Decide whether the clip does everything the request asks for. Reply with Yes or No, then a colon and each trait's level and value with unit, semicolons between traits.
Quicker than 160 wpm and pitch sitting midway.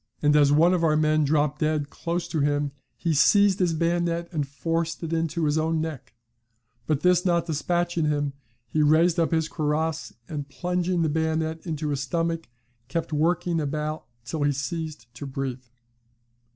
Yes: average, 175 wpm; medium, 160 Hz